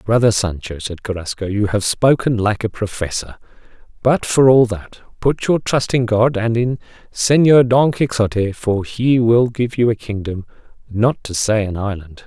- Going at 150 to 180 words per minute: Yes, average, 175 wpm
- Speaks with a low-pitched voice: Yes, low, 110 Hz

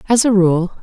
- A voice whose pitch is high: Yes, high, 195 Hz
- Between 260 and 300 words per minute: No, fast, 220 wpm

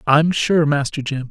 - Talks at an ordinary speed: Yes, average, 185 wpm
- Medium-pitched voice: Yes, medium, 145 Hz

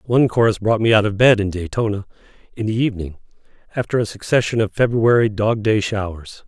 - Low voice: Yes, low, 110 Hz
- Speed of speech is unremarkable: Yes, average, 165 wpm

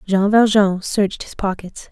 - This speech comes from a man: No, female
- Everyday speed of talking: Yes, average, 155 wpm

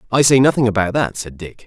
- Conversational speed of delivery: No, fast, 255 wpm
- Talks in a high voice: No, low, 115 Hz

